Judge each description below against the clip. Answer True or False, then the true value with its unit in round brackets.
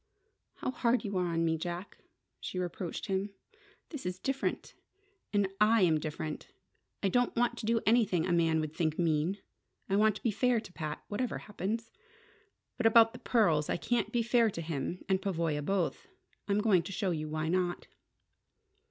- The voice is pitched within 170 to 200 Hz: True (190 Hz)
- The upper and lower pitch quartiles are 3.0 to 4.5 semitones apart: False (5.3 semitones)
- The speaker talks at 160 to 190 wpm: True (180 wpm)